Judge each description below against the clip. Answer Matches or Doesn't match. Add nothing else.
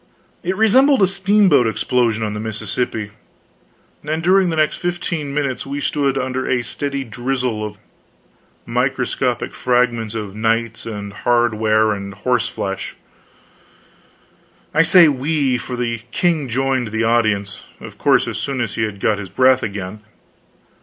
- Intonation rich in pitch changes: Doesn't match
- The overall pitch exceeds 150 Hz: Doesn't match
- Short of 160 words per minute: Matches